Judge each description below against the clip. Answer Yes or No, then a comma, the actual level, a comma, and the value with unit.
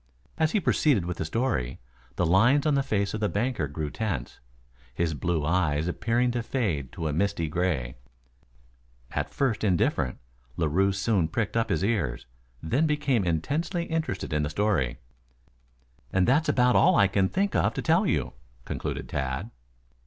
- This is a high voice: No, low, 100 Hz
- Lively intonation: Yes, wide, 7.8 semitones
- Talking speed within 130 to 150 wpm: No, average, 165 wpm